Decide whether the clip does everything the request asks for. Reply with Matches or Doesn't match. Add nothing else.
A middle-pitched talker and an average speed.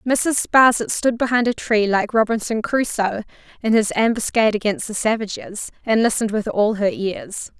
Doesn't match